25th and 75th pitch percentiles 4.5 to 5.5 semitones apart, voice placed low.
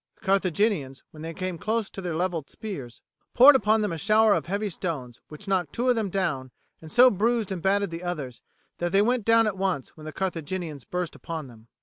No: average, 4.9 semitones; medium, 185 Hz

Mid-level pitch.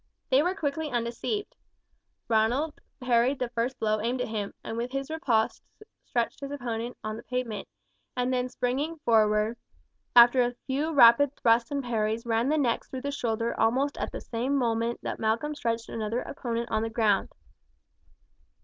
No: high, 240 Hz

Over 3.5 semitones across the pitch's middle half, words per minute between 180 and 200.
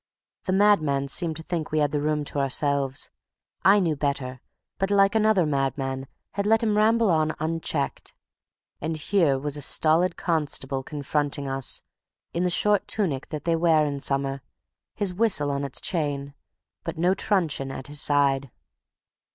No: average, 4.5 semitones; average, 160 wpm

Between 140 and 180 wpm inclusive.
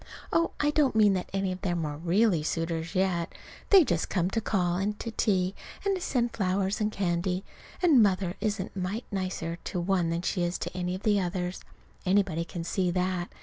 No: fast, 205 wpm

